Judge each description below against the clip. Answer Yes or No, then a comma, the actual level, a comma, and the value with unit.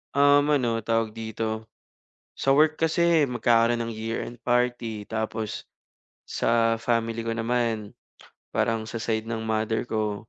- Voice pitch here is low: Yes, low, 115 Hz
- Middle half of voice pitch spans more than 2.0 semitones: No, narrow, 1.7 semitones